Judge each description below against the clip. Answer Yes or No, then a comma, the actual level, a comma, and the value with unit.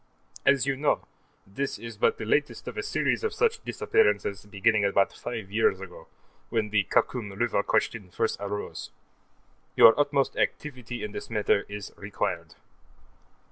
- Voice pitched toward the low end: Yes, low, 110 Hz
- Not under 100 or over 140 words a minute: No, average, 150 wpm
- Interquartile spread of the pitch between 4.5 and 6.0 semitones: Yes, average, 5.2 semitones